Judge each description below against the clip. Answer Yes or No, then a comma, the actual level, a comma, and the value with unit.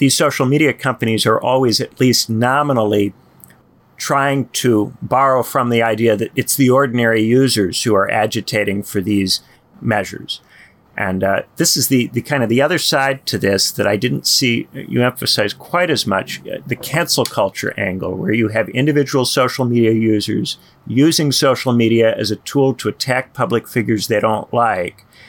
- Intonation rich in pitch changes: No, average, 4.1 semitones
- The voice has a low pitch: Yes, low, 120 Hz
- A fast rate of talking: No, average, 170 wpm